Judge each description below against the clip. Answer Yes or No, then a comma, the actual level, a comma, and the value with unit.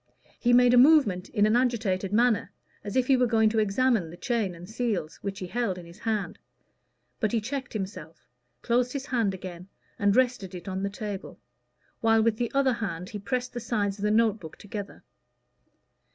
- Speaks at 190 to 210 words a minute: Yes, average, 195 wpm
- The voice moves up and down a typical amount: Yes, average, 3.9 semitones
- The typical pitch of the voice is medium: No, high, 215 Hz